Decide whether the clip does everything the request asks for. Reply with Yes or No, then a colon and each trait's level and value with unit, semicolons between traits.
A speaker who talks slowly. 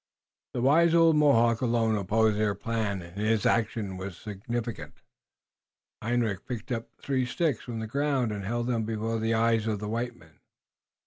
No: average, 170 wpm